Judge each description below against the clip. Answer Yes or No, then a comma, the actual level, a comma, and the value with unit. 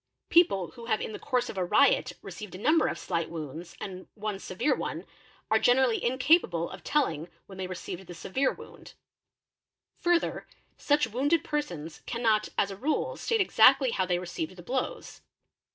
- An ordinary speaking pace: Yes, average, 170 wpm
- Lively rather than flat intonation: Yes, wide, 7.0 semitones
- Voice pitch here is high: Yes, high, 215 Hz